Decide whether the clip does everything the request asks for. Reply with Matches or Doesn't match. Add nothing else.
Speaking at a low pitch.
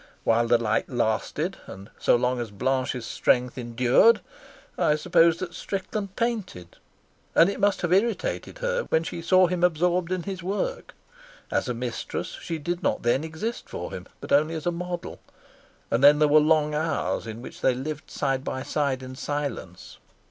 Doesn't match